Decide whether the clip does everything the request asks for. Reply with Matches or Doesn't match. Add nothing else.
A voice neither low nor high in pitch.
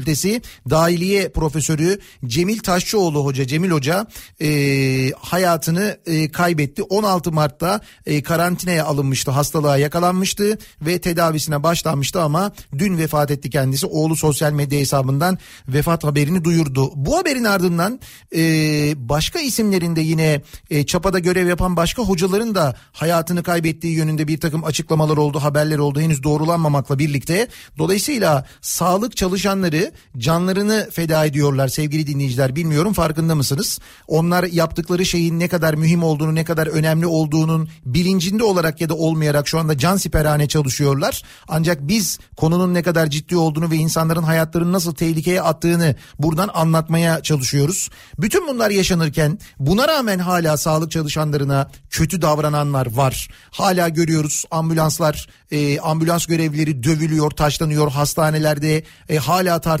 Matches